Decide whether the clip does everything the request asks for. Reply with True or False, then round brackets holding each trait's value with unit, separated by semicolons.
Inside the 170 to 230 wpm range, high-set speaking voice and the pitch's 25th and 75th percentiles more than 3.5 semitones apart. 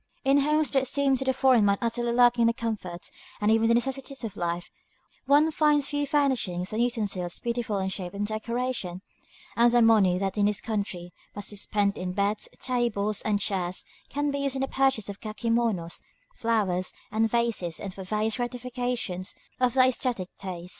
True (190 wpm; 225 Hz; 4.1 semitones)